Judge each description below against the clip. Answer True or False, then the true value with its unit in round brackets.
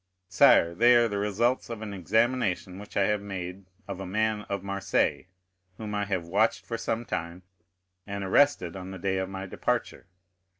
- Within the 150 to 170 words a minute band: False (180 wpm)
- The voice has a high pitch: False (100 Hz)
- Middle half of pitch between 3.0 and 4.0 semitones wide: False (2.6 semitones)